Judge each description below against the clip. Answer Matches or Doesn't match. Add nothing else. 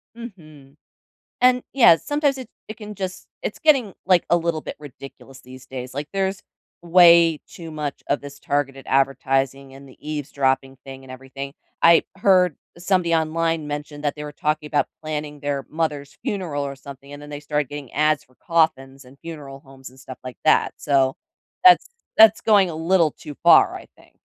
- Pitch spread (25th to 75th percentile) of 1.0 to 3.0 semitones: Doesn't match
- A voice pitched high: Doesn't match